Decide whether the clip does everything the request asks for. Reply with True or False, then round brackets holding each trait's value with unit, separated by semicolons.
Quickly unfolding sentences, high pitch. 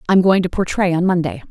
False (280 wpm; 175 Hz)